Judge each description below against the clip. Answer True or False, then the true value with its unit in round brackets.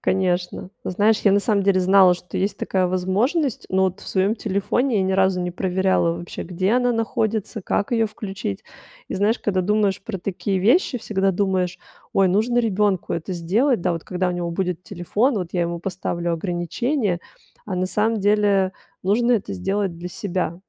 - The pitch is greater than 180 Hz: True (190 Hz)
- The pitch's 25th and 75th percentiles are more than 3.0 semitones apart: False (2.7 semitones)